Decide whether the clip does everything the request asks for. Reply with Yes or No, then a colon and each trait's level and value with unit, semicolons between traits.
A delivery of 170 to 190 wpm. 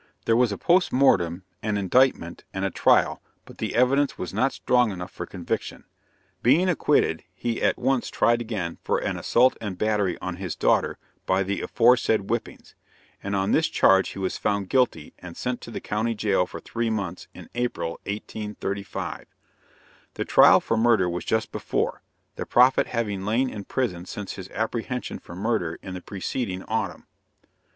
Yes: average, 175 wpm